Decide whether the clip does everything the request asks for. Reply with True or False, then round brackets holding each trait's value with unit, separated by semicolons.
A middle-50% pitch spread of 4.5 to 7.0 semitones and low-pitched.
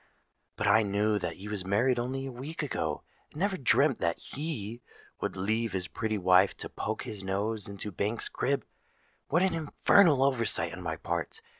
True (5.3 semitones; 110 Hz)